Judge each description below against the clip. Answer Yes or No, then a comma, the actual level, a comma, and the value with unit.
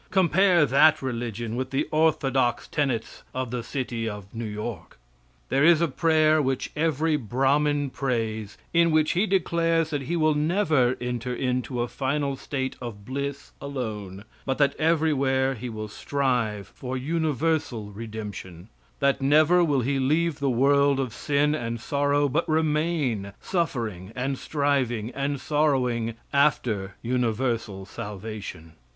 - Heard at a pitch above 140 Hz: No, low, 135 Hz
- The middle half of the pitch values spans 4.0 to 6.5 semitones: Yes, average, 4.6 semitones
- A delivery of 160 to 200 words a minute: No, average, 140 wpm